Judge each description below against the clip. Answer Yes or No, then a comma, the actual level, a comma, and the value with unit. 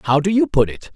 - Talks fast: Yes, fast, 315 wpm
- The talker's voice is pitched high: No, medium, 160 Hz